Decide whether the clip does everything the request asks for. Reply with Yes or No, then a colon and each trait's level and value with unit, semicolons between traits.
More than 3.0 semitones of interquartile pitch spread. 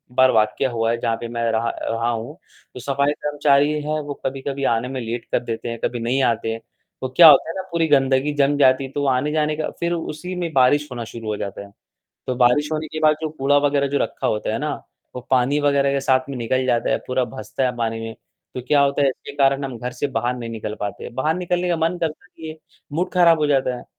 Yes: average, 3.8 semitones